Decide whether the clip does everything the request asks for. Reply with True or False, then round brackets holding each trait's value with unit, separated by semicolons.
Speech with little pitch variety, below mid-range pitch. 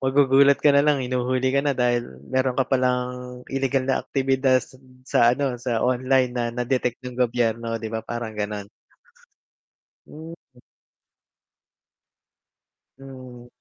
True (1.5 semitones; 130 Hz)